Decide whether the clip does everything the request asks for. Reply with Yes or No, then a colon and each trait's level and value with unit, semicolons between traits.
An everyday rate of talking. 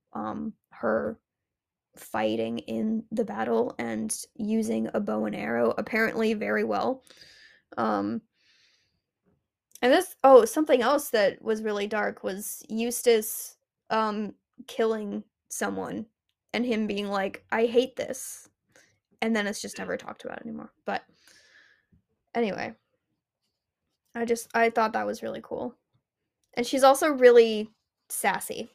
No: slow, 125 wpm